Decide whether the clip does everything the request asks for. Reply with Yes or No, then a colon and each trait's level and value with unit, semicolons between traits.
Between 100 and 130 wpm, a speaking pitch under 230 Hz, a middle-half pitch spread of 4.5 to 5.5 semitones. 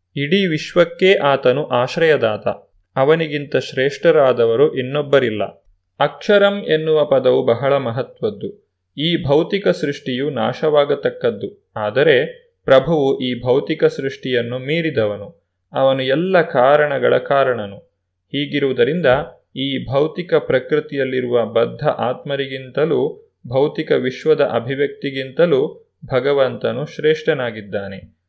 No: average, 80 wpm; medium, 140 Hz; average, 5.0 semitones